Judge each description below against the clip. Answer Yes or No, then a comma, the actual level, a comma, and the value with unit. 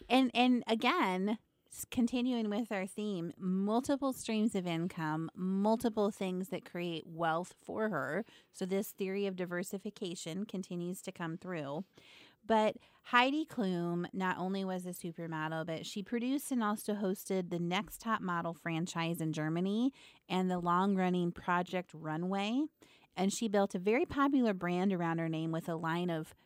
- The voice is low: No, high, 190 Hz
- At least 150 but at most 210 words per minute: Yes, average, 155 wpm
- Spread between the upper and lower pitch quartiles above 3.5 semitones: Yes, average, 3.9 semitones